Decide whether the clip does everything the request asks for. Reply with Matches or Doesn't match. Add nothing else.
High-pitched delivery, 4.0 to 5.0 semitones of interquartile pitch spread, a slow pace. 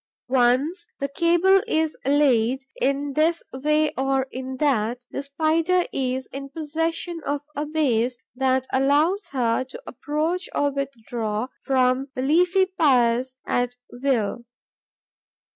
Doesn't match